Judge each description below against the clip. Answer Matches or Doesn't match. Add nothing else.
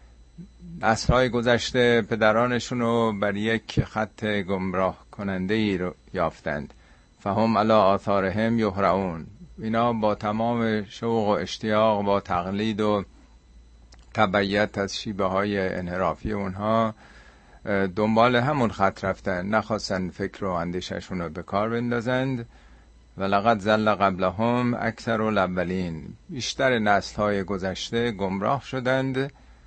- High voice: Doesn't match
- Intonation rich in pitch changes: Doesn't match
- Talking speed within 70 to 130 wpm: Matches